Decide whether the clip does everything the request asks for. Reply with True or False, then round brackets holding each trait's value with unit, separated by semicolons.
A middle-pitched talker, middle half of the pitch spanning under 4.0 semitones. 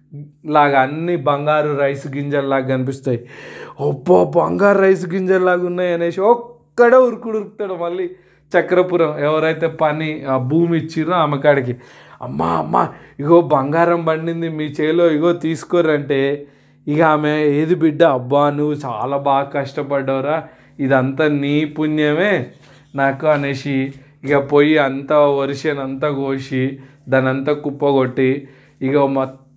True (150 Hz; 3.1 semitones)